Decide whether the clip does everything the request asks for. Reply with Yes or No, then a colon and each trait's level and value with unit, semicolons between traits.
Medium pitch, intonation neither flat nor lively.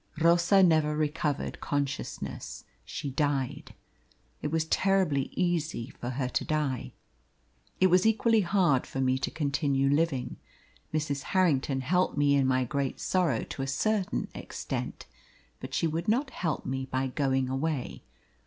Yes: medium, 150 Hz; average, 4.3 semitones